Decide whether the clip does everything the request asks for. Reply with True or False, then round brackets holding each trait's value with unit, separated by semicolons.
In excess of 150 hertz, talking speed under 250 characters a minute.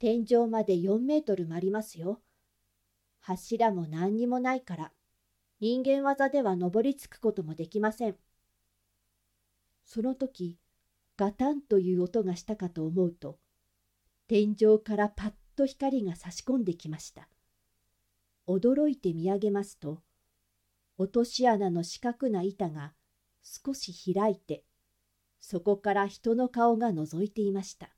True (185 Hz; 240 characters per minute)